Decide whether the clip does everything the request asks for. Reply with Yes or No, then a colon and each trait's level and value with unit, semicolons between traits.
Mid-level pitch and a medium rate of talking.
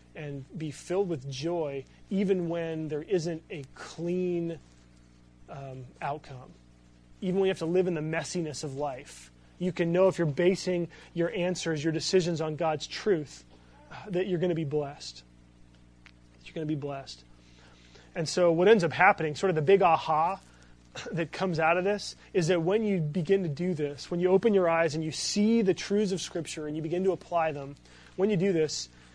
Yes: medium, 160 Hz; average, 195 wpm